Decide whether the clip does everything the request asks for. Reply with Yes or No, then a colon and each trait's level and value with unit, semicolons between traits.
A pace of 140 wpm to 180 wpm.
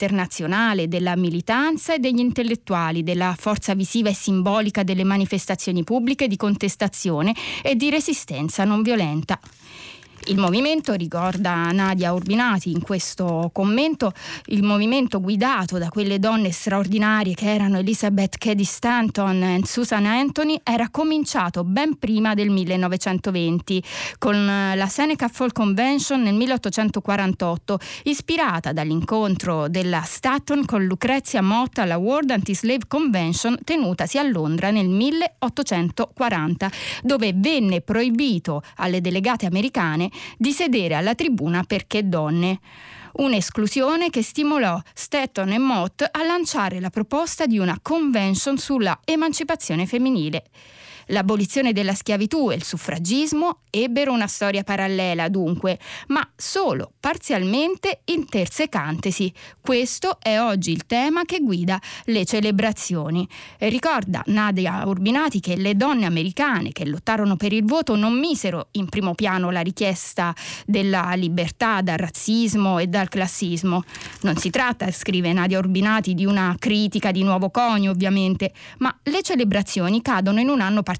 No: average, 125 wpm